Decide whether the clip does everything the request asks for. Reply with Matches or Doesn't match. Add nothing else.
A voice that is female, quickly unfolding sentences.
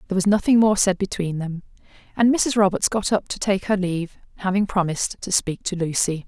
Matches